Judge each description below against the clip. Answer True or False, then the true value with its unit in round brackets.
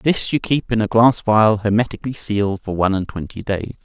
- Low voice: True (110 Hz)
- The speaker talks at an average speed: False (220 wpm)